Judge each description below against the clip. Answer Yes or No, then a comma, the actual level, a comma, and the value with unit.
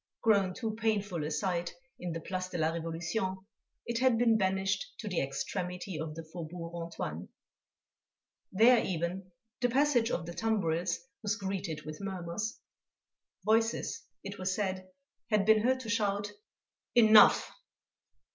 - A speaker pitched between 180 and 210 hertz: Yes, high, 190 Hz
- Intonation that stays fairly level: No, average, 4.2 semitones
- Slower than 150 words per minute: Yes, average, 140 wpm